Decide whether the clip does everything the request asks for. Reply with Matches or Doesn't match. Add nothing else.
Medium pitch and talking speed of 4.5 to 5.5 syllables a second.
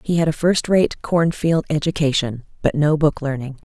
Matches